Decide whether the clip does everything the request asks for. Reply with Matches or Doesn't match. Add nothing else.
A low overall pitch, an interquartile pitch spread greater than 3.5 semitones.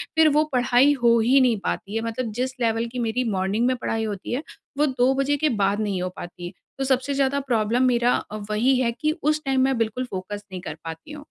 Doesn't match